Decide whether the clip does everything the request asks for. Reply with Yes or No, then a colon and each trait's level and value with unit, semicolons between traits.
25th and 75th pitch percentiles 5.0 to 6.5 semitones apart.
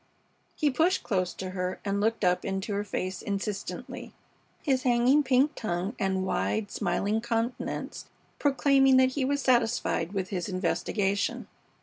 Yes: average, 5.3 semitones